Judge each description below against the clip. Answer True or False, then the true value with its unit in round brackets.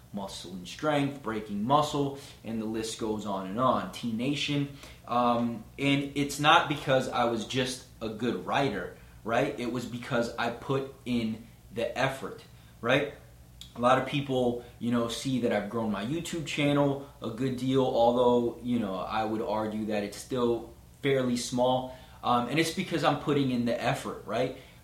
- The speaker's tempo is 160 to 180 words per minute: True (175 wpm)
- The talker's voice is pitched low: True (120 Hz)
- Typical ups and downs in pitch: True (3.7 semitones)